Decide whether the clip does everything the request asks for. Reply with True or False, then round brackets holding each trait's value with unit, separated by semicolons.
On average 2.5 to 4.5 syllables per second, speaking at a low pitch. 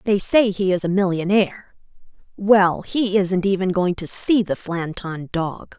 False (4.2 syllables/s; 190 Hz)